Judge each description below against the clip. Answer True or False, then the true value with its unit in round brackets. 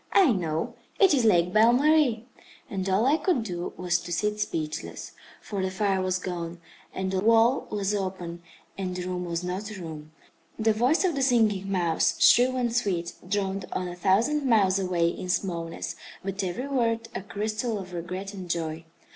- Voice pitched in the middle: False (195 Hz)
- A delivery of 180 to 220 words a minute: True (185 wpm)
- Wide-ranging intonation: False (4.1 semitones)